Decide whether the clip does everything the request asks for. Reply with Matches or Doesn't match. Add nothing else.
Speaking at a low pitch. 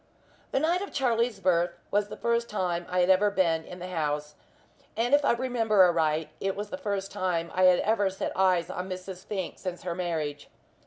Doesn't match